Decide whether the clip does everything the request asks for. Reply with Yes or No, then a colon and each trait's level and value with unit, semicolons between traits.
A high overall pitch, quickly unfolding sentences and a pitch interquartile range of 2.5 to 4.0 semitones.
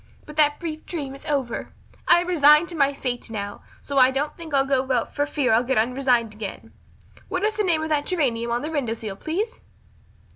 No: very high, 280 Hz; fast, 220 wpm; average, 4.4 semitones